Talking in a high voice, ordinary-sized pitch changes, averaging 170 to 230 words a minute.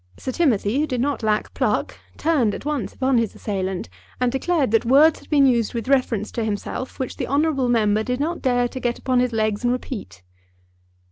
Yes: very high, 250 Hz; average, 3.7 semitones; fast, 205 wpm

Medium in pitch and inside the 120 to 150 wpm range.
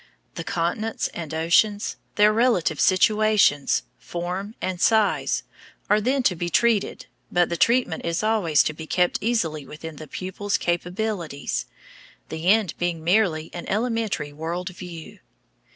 Yes: medium, 180 Hz; slow, 135 wpm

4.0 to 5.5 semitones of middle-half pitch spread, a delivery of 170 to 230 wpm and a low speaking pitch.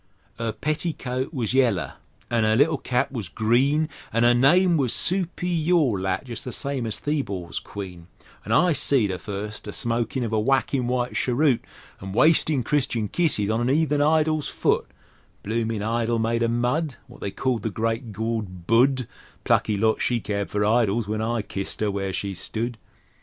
Yes: average, 4.3 semitones; average, 180 wpm; low, 120 Hz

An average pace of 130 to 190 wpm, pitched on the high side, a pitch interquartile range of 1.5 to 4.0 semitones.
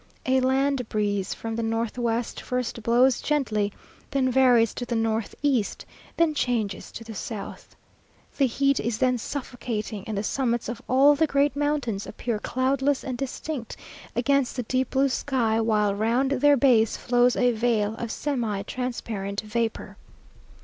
Yes: average, 155 wpm; high, 240 Hz; average, 3.1 semitones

